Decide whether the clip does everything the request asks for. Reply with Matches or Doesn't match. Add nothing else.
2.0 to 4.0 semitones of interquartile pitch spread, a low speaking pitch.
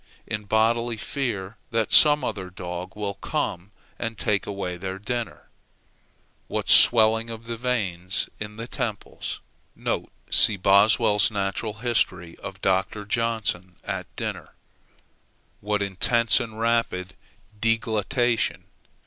Matches